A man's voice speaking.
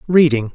Yes: male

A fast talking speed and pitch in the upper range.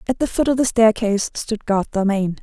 Yes: fast, 225 wpm; high, 215 Hz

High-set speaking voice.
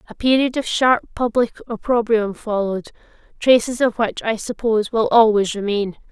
Yes: high, 225 Hz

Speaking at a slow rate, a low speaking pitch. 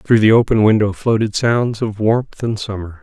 No: average, 200 wpm; low, 110 Hz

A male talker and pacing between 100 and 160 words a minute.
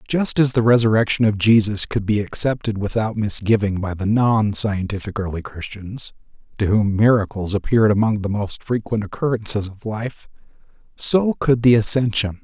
Yes: male; average, 155 wpm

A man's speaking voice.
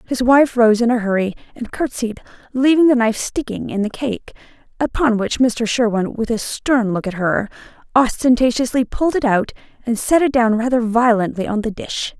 No: female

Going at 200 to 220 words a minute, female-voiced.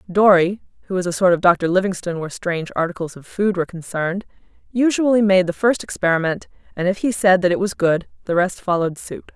Yes: fast, 205 wpm; female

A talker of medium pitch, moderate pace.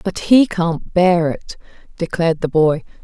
Yes: medium, 170 Hz; average, 160 wpm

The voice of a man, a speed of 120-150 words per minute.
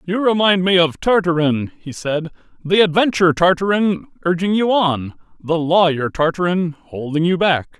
Yes: male; average, 145 wpm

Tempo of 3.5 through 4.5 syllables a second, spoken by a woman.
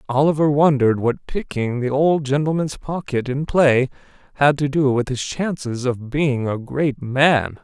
No: 4.3 syllables/s; male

